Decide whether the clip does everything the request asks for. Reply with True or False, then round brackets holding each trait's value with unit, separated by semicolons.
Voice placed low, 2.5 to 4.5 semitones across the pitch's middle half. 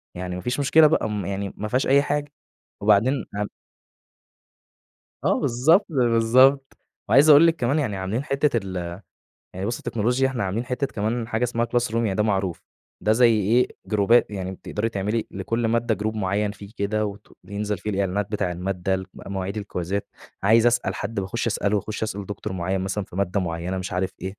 True (105 Hz; 3.7 semitones)